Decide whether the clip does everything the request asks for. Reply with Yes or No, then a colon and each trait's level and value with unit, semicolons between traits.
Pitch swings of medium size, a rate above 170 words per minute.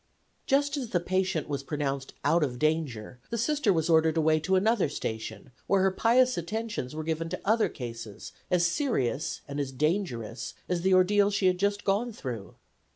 No: wide, 6.2 semitones; average, 180 wpm